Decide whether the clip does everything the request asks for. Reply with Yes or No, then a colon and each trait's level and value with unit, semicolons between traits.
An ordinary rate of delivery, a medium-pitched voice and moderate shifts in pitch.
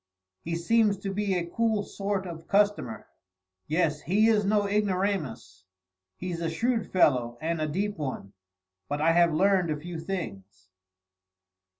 Yes: average, 155 wpm; medium, 175 Hz; average, 4.6 semitones